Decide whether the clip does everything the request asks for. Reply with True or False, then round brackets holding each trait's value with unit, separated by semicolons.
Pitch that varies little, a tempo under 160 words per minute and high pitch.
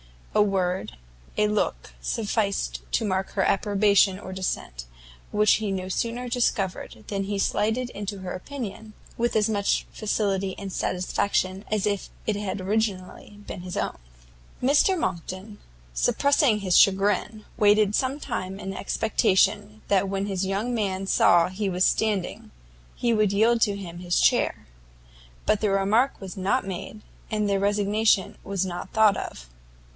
True (2.2 semitones; 150 wpm; 200 Hz)